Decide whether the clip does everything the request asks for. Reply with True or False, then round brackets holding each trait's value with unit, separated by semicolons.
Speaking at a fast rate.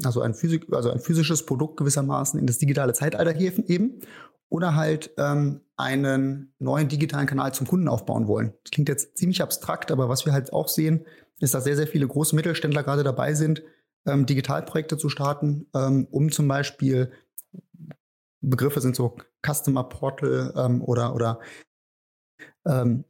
False (165 wpm)